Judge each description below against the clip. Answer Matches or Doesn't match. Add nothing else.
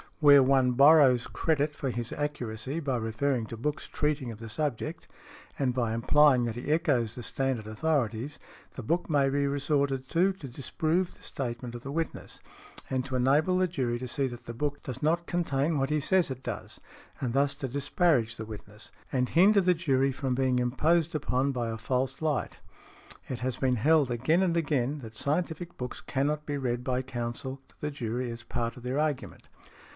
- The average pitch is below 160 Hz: Matches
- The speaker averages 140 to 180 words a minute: Doesn't match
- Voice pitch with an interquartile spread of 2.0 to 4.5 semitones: Matches